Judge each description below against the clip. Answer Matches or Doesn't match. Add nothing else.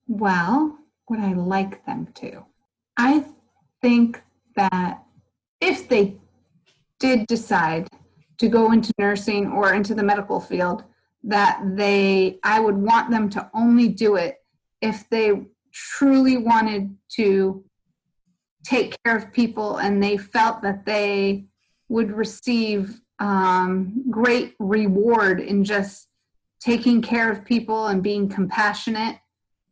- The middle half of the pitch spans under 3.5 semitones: Matches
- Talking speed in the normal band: Doesn't match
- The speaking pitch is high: Matches